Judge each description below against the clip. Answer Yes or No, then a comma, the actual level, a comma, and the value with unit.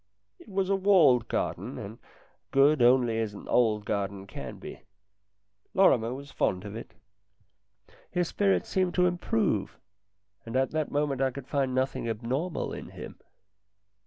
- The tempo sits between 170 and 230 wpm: No, average, 150 wpm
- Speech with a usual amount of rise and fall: No, wide, 7.3 semitones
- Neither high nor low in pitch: No, low, 130 Hz